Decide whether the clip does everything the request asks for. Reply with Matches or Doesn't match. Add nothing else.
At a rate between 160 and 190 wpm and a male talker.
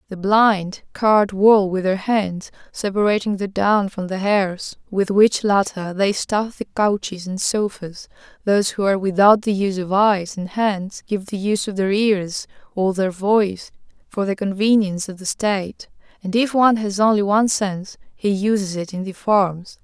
Doesn't match